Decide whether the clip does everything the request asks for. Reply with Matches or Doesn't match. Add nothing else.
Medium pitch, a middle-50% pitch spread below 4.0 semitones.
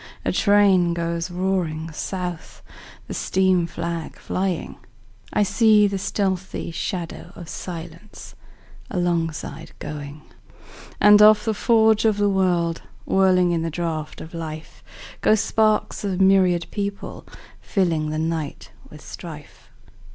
Matches